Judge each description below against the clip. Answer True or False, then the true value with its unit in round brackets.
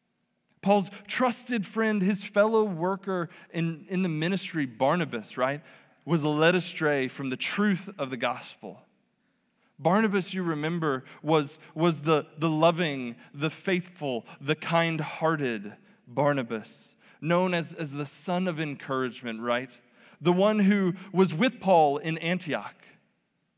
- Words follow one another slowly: True (130 wpm)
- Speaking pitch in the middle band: True (165 Hz)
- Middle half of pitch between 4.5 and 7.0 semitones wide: True (4.8 semitones)